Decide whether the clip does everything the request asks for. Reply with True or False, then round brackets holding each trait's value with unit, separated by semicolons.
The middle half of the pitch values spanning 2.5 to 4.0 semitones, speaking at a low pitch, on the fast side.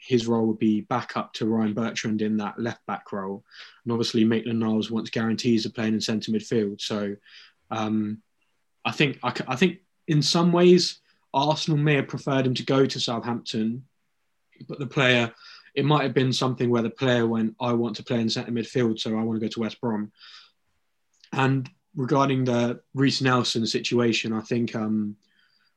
False (3.2 semitones; 120 Hz; 180 wpm)